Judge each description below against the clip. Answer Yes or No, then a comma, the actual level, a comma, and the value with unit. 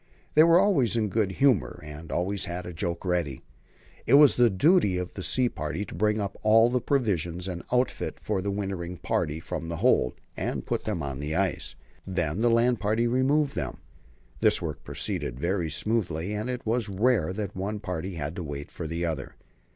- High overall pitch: No, very low, 95 Hz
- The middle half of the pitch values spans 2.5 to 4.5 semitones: No, wide, 5.5 semitones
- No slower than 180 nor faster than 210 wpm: Yes, average, 200 wpm